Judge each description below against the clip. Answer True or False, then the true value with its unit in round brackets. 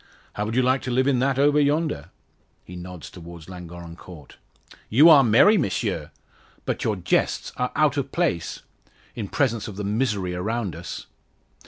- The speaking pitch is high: False (110 Hz)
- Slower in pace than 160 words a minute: False (170 wpm)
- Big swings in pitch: True (7.3 semitones)